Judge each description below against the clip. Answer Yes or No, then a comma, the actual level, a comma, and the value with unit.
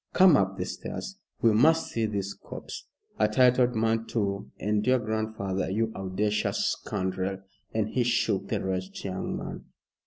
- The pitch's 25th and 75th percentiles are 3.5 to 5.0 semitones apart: No, average, 3.0 semitones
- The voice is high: No, low, 105 Hz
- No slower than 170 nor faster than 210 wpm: No, average, 155 wpm